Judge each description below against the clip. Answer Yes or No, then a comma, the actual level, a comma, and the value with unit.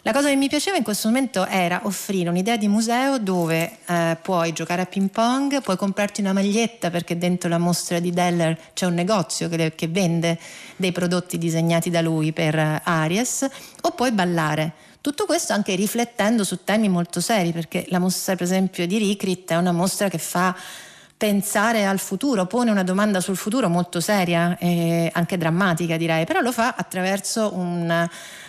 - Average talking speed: No, fast, 180 wpm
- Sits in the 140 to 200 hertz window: Yes, medium, 185 Hz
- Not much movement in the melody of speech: No, average, 3.4 semitones